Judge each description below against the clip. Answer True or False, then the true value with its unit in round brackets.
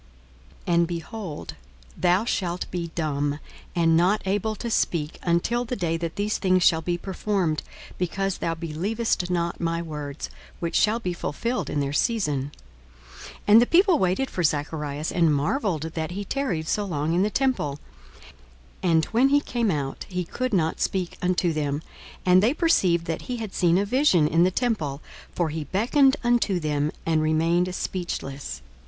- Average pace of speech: True (170 wpm)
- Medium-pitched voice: True (175 Hz)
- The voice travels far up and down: False (4.7 semitones)